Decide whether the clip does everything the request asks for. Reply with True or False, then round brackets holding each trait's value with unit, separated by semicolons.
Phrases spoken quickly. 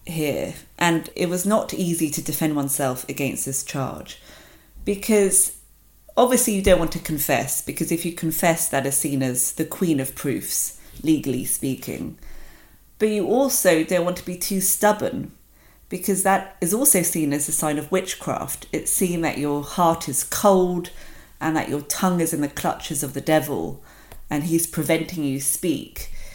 False (170 wpm)